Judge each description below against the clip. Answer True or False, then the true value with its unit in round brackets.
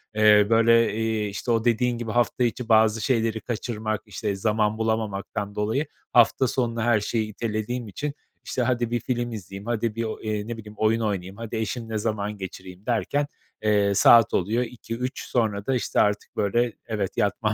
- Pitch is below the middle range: True (110 Hz)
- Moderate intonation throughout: False (2.0 semitones)